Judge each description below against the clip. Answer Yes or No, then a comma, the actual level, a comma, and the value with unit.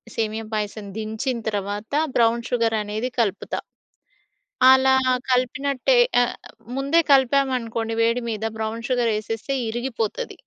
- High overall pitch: Yes, high, 230 Hz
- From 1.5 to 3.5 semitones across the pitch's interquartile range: Yes, average, 2.8 semitones